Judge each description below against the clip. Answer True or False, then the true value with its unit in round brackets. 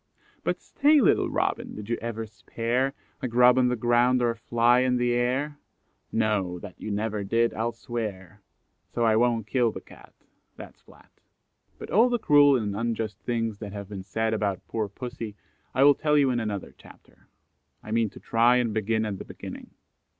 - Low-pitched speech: True (115 Hz)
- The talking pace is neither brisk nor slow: True (190 wpm)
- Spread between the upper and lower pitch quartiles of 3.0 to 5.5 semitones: False (2.5 semitones)